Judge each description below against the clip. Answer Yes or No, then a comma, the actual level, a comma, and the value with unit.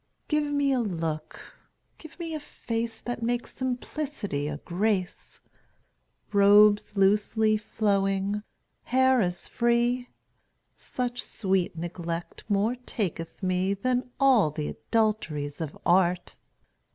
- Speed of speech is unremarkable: No, slow, 110 wpm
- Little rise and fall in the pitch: No, average, 5.1 semitones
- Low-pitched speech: No, high, 210 Hz